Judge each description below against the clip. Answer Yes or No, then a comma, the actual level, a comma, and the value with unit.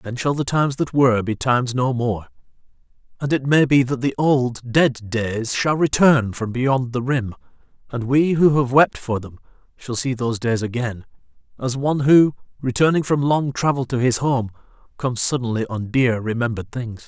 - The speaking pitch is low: Yes, low, 125 Hz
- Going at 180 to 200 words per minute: Yes, average, 185 wpm